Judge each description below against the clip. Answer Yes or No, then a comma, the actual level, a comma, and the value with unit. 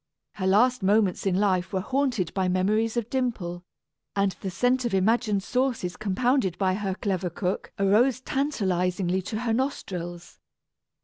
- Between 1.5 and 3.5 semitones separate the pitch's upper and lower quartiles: No, average, 4.6 semitones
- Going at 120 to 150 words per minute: Yes, average, 145 wpm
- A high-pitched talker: Yes, high, 200 Hz